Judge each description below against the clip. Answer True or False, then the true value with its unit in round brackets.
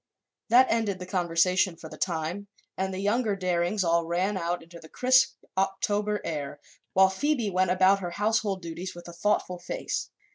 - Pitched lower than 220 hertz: True (185 Hz)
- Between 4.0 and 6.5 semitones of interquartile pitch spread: False (3.0 semitones)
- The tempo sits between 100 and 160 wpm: False (175 wpm)